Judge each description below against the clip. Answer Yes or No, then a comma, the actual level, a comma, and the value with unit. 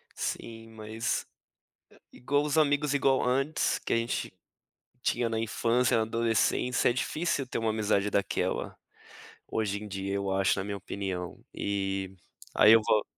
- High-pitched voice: No, low, 110 Hz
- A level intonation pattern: No, average, 3.9 semitones